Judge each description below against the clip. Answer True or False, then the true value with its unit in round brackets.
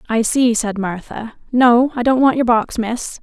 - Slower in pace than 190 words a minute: False (205 wpm)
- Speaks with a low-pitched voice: False (235 Hz)